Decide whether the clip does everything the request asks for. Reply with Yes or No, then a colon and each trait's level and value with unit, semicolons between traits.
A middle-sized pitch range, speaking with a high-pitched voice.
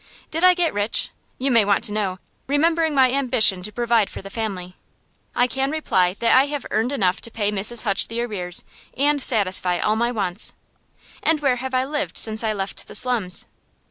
Yes: average, 5.0 semitones; high, 230 Hz